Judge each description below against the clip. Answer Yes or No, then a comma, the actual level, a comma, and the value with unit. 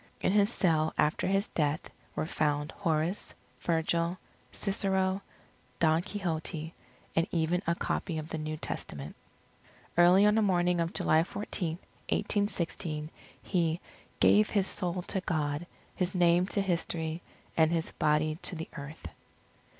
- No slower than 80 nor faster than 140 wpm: Yes, slow, 135 wpm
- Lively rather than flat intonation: No, average, 3.0 semitones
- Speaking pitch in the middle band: Yes, medium, 170 Hz